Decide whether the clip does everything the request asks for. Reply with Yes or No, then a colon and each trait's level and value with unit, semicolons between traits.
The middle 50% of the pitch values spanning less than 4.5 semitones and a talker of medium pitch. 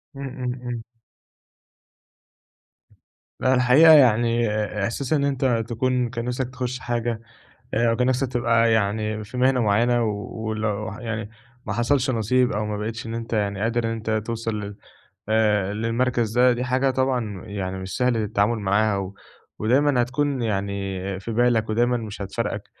No: average, 2.8 semitones; low, 115 Hz